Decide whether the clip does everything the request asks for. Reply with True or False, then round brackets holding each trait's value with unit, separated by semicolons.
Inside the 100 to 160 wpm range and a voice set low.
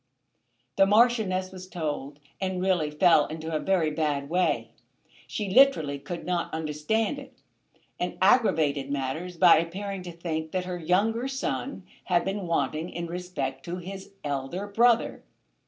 False (145 wpm; 180 Hz)